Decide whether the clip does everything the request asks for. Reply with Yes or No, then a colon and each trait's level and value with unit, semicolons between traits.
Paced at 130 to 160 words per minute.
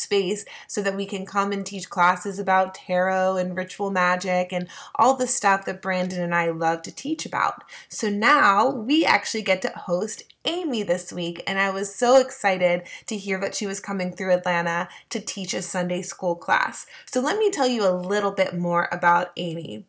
No: average, 200 wpm